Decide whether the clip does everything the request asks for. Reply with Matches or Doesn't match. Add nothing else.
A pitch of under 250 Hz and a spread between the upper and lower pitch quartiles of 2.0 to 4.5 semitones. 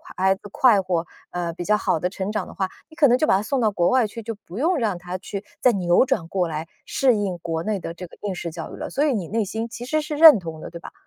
Doesn't match